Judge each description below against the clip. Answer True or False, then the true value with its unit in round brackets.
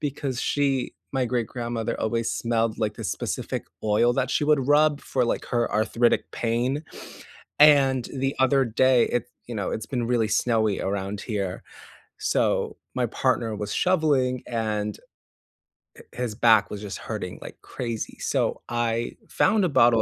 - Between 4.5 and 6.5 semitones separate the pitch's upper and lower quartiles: False (3.0 semitones)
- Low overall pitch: True (120 Hz)